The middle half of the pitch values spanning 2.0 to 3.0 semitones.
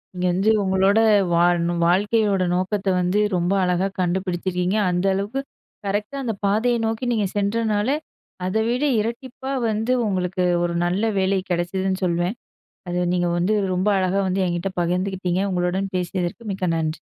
Yes: average, 2.7 semitones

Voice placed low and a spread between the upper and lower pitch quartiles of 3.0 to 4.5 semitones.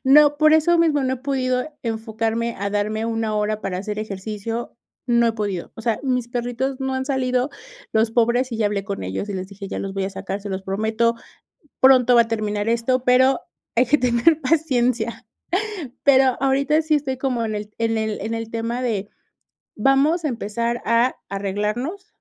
No: high, 235 Hz; average, 3.6 semitones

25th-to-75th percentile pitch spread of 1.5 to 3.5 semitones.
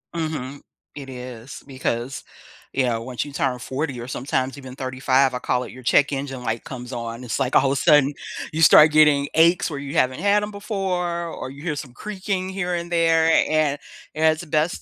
No: average, 4.0 semitones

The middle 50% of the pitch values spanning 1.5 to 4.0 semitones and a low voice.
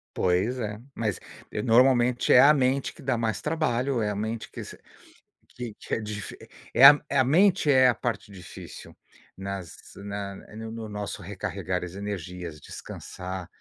No: average, 4.5 semitones; low, 110 Hz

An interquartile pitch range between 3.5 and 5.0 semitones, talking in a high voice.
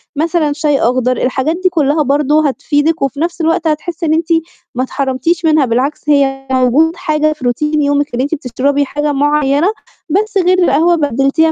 No: average, 2.8 semitones; very high, 295 Hz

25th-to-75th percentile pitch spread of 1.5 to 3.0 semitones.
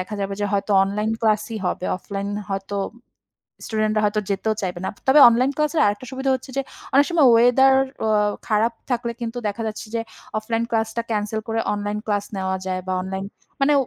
Yes: average, 2.7 semitones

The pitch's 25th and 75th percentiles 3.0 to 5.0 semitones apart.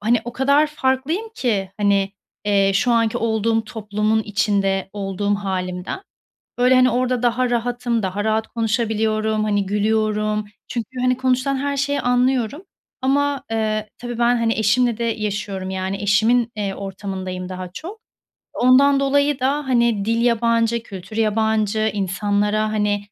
Yes: average, 3.3 semitones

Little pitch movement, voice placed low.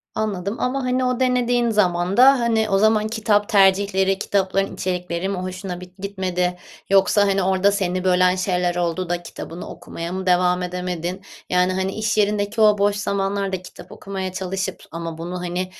No: narrow, 2.2 semitones; high, 190 Hz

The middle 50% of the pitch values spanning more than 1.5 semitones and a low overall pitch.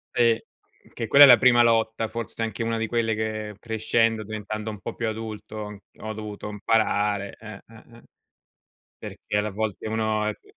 No: narrow, 1.2 semitones; low, 110 Hz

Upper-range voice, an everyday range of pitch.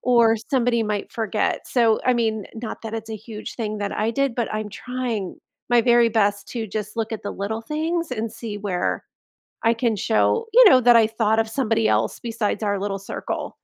No: high, 225 Hz; narrow, 2.0 semitones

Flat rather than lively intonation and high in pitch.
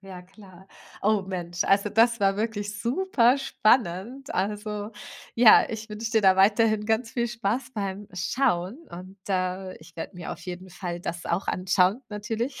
No: average, 3.5 semitones; high, 205 Hz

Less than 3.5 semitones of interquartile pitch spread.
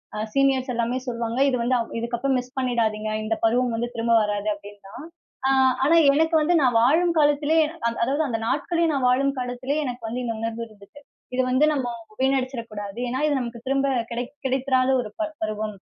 Yes: average, 3.1 semitones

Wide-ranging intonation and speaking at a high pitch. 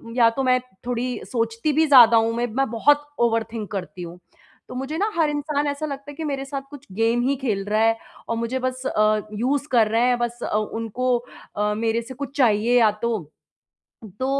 No: average, 3.3 semitones; high, 240 Hz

